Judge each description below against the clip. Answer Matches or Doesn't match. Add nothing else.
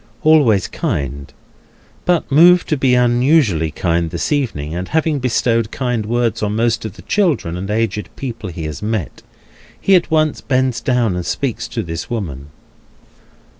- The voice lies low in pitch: Matches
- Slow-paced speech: Doesn't match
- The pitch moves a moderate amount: Doesn't match